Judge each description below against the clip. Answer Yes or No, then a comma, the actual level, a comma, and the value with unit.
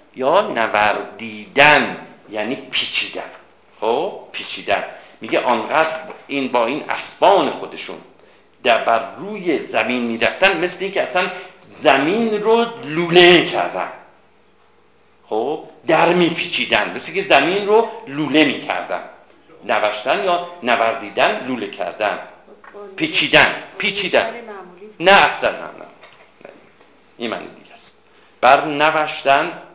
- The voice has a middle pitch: Yes, medium, 170 Hz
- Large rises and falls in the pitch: Yes, wide, 5.8 semitones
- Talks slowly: Yes, slow, 100 wpm